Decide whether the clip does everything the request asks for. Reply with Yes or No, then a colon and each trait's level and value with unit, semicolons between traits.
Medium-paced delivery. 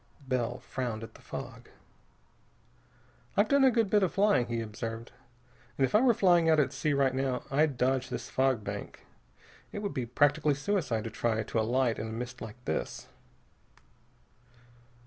Yes: average, 170 wpm